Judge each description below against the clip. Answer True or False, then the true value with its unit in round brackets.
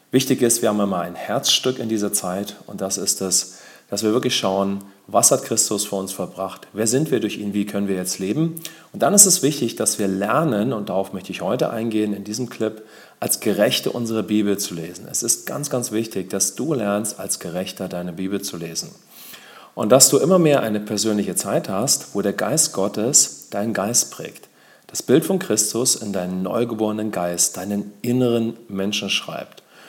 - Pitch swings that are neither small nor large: True (3.1 semitones)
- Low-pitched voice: True (105 Hz)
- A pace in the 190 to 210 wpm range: True (200 wpm)